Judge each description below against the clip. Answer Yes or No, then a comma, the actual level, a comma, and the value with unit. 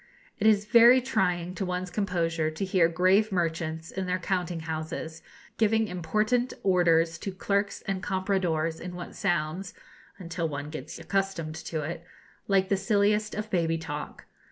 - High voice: No, medium, 180 Hz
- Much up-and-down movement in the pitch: No, average, 3.3 semitones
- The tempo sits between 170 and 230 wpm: No, average, 155 wpm